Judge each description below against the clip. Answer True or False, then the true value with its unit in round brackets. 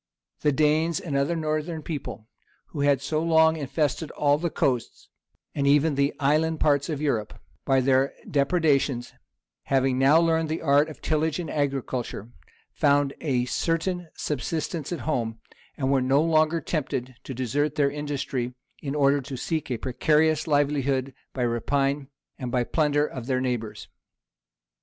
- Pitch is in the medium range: True (145 Hz)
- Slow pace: False (155 wpm)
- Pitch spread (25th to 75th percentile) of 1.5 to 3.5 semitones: True (2.7 semitones)